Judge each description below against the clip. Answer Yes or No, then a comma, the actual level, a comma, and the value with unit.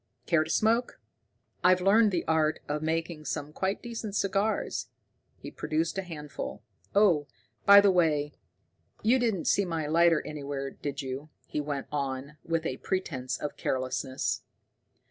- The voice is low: No, medium, 160 Hz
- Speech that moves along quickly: No, average, 145 wpm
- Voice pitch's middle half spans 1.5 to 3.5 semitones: No, average, 4.7 semitones